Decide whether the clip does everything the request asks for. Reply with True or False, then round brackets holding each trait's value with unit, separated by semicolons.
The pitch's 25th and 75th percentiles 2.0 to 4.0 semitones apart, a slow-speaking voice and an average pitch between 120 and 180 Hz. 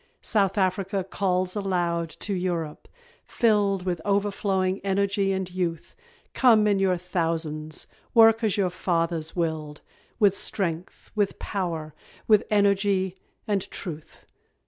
False (2.8 semitones; 120 wpm; 190 Hz)